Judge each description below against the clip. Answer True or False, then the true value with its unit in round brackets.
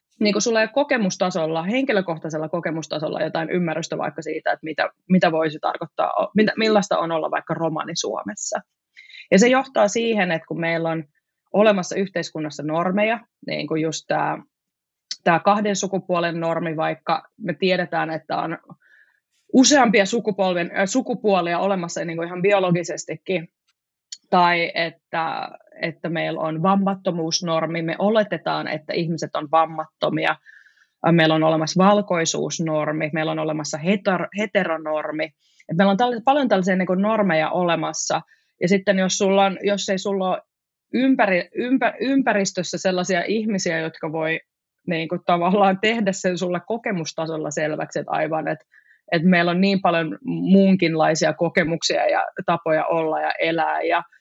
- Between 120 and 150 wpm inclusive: True (135 wpm)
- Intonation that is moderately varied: True (3.7 semitones)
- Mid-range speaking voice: True (180 Hz)